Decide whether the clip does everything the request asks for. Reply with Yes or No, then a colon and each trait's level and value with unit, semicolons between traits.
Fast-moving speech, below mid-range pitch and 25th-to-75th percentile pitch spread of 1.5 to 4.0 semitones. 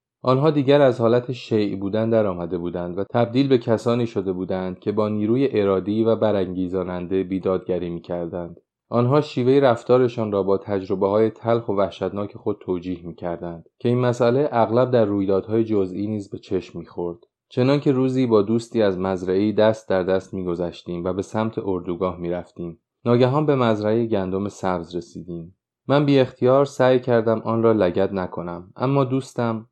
No: fast, 170 wpm; low, 105 Hz; average, 4.5 semitones